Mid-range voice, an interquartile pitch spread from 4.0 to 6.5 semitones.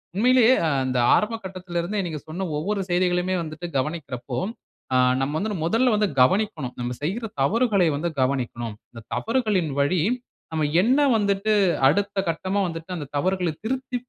Yes: medium, 180 Hz; wide, 5.6 semitones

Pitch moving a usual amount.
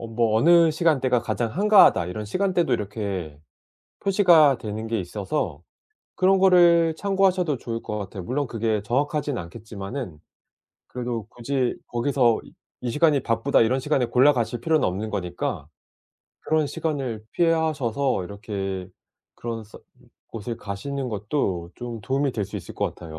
No: wide, 6.1 semitones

